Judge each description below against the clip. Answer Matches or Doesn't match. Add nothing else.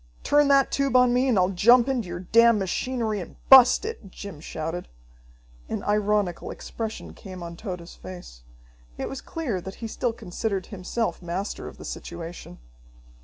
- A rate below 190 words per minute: Matches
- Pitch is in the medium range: Doesn't match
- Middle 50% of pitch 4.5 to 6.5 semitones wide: Matches